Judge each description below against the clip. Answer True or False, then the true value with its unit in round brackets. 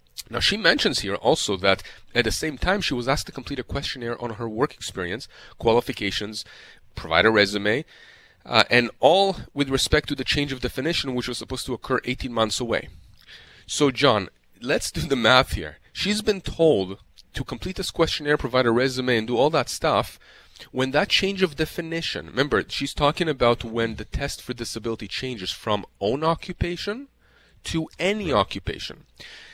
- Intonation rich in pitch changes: True (6.0 semitones)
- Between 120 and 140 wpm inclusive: False (175 wpm)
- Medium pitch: False (130 Hz)